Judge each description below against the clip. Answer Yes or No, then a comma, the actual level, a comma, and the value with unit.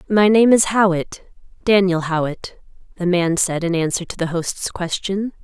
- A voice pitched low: No, medium, 185 Hz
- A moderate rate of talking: Yes, average, 165 wpm